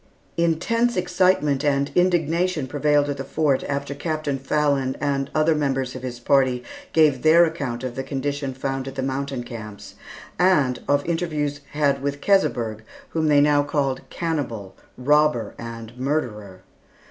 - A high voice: No, medium, 140 Hz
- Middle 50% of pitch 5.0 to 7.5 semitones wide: No, average, 2.9 semitones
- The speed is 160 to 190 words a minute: No, average, 145 wpm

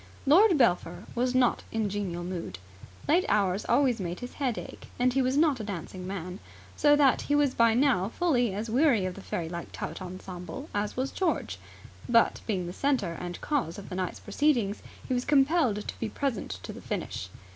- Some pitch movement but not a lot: No, wide, 6.5 semitones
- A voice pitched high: Yes, high, 230 Hz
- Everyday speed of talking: Yes, average, 195 wpm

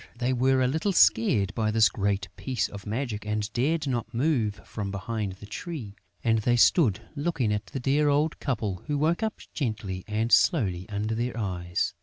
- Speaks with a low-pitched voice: Yes, low, 115 Hz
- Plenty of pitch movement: No, average, 4.7 semitones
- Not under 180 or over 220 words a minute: Yes, average, 190 wpm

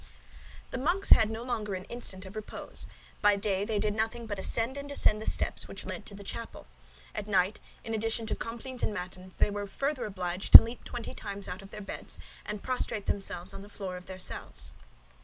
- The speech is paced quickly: Yes, fast, 215 wpm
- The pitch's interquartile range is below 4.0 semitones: Yes, average, 2.8 semitones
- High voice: Yes, high, 210 Hz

